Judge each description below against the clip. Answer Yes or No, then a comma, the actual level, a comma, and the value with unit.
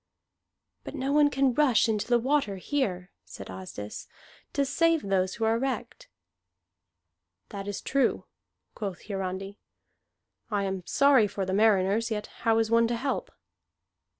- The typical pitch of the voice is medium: No, high, 220 Hz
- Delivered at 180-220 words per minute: No, average, 145 wpm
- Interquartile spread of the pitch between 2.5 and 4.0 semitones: No, average, 5.2 semitones